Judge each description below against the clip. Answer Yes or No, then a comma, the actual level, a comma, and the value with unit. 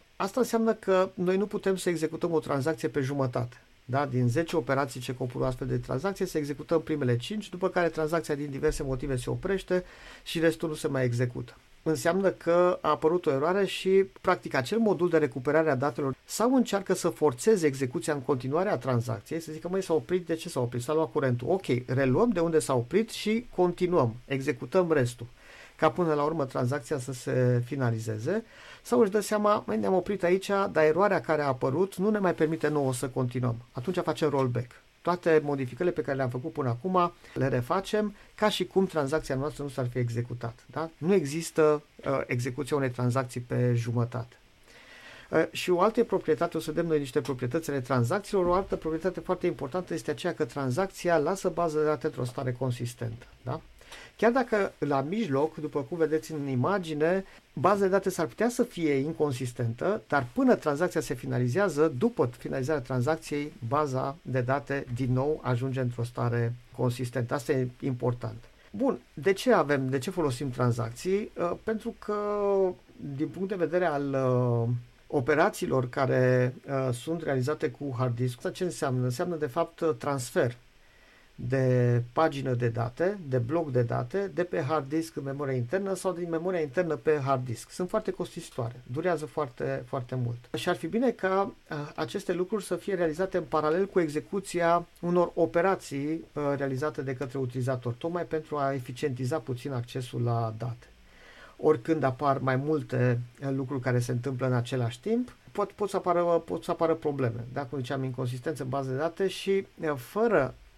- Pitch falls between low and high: Yes, medium, 150 Hz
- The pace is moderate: No, fast, 175 wpm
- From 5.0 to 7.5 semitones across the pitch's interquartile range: Yes, average, 5.3 semitones